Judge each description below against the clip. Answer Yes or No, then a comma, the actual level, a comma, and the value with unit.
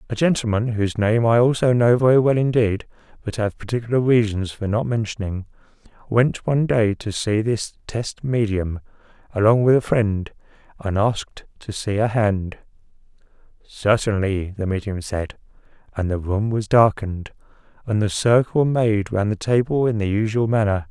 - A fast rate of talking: No, average, 160 wpm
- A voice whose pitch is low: Yes, low, 110 Hz